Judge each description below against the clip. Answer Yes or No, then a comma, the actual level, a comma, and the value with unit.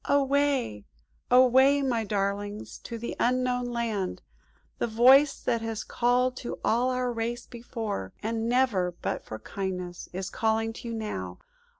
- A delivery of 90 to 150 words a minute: Yes, average, 140 wpm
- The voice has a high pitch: Yes, high, 230 Hz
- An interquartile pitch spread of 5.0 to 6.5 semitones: No, average, 3.5 semitones